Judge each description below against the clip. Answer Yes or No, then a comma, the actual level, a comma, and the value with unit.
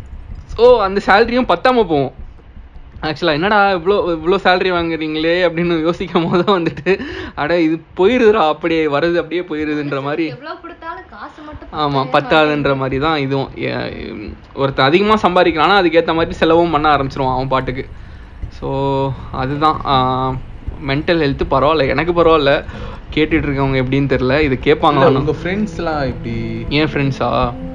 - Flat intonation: No, average, 4.4 semitones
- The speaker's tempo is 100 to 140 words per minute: Yes, average, 120 wpm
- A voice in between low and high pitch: Yes, medium, 155 Hz